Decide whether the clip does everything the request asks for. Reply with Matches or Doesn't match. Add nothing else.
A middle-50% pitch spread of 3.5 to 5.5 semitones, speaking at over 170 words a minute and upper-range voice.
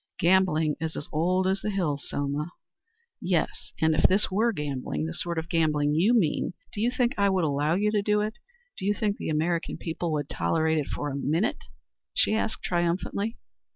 Doesn't match